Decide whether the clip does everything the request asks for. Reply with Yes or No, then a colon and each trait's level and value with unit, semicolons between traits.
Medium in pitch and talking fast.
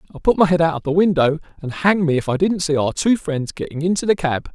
Yes: medium, 165 Hz; fast, 290 wpm